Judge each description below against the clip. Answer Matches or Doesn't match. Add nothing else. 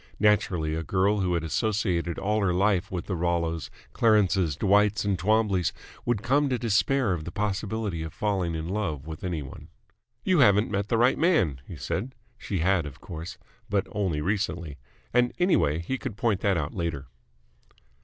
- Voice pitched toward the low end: Matches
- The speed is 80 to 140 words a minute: Doesn't match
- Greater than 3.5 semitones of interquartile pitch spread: Matches